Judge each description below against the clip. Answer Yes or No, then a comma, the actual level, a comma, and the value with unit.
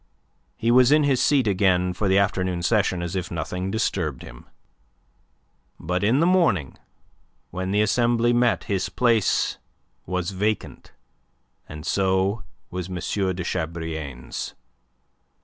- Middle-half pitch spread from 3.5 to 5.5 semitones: Yes, average, 4.2 semitones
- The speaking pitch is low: Yes, very low, 95 Hz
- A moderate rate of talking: No, slow, 130 wpm